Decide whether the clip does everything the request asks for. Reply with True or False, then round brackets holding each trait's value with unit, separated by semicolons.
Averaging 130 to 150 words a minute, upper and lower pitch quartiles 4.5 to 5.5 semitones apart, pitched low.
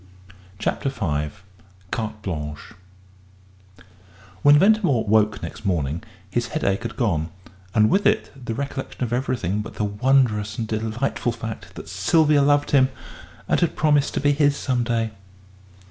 True (145 wpm; 5.0 semitones; 115 Hz)